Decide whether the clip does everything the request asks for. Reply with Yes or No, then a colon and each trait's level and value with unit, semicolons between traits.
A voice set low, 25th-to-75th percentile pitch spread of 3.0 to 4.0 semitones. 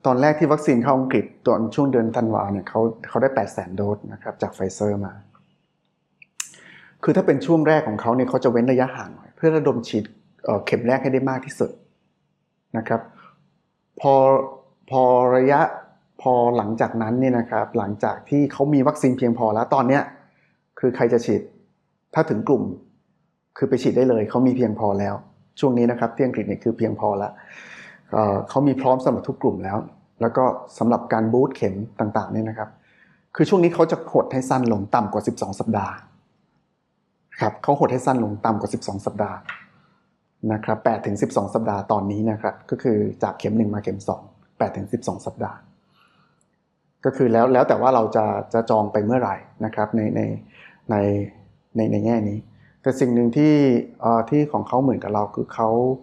Yes: low, 115 Hz; average, 3.5 semitones